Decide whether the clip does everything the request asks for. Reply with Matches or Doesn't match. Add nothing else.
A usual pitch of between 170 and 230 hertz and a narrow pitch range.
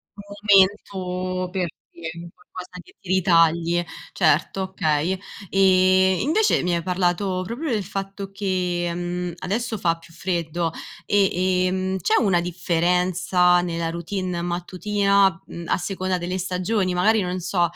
Matches